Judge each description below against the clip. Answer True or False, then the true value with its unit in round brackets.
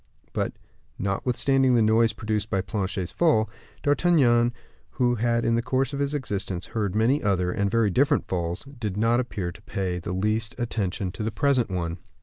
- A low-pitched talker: True (110 Hz)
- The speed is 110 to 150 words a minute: False (175 wpm)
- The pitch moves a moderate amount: True (4.2 semitones)